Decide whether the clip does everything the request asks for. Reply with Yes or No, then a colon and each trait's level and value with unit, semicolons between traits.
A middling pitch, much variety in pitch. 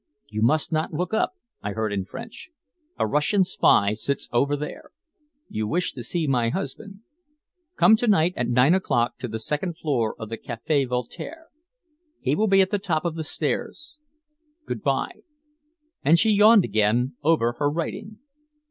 Yes: medium, 150 Hz; wide, 8.1 semitones